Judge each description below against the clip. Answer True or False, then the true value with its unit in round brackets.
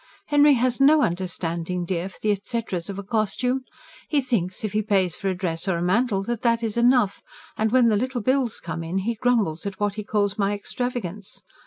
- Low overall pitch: False (210 Hz)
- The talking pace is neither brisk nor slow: False (210 wpm)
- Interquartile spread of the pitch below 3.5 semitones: False (4.4 semitones)